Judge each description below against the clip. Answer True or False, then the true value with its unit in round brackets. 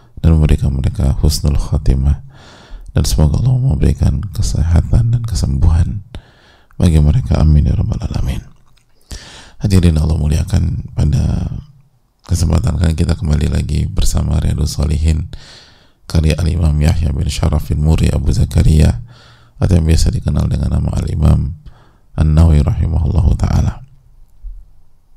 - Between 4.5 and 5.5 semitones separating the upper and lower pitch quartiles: False (3.5 semitones)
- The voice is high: False (85 Hz)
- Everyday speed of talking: False (120 wpm)